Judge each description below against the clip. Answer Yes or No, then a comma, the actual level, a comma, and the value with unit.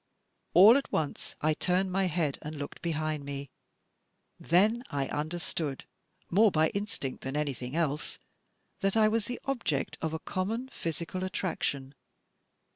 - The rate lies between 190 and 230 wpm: No, average, 140 wpm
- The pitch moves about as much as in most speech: Yes, average, 4.9 semitones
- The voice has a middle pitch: Yes, medium, 165 Hz